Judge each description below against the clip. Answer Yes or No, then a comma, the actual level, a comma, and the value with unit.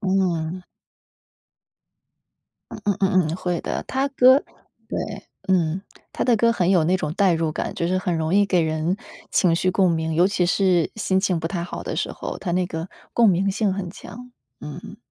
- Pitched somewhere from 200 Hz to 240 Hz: No, medium, 185 Hz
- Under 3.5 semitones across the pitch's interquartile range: Yes, average, 2.8 semitones